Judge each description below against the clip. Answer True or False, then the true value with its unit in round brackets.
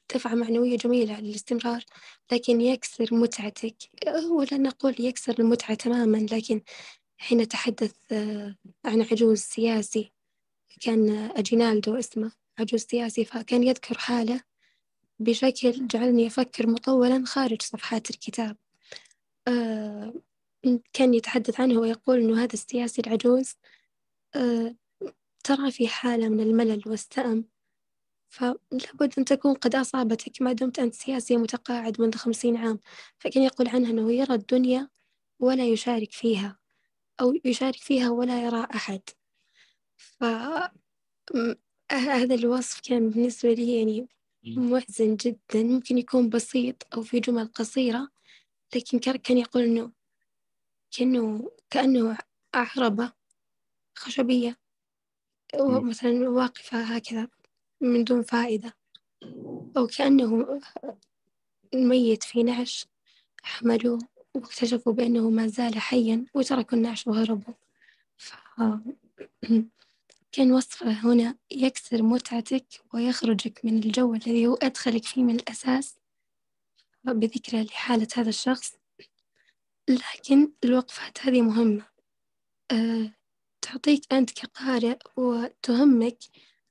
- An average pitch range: False (1.9 semitones)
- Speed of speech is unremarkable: True (100 wpm)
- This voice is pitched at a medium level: False (240 Hz)